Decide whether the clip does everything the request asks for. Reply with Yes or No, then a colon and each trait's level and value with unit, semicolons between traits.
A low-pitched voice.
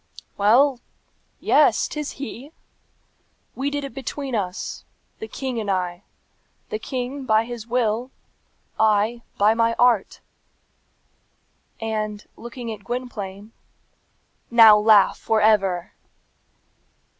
No: high, 225 Hz